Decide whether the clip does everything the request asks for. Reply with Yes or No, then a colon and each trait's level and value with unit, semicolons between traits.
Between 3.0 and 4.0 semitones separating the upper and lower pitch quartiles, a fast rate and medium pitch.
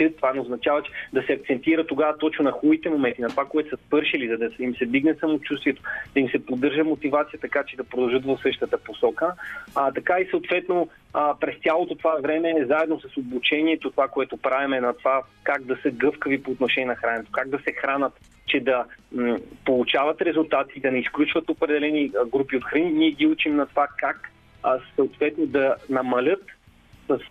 Yes: average, 3.3 semitones; fast, 195 wpm; medium, 145 Hz